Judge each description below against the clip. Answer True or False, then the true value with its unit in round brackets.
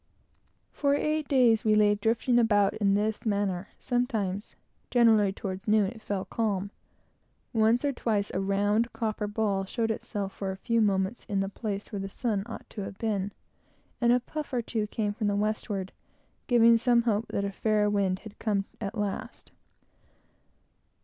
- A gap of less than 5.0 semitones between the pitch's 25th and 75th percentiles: True (2.4 semitones)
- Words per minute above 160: True (170 wpm)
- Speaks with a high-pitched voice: True (210 Hz)